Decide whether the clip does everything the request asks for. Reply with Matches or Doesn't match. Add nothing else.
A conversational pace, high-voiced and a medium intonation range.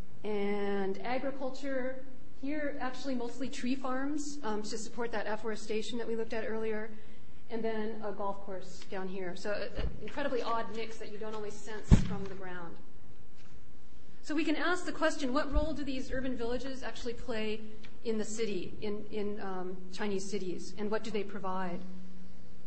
Matches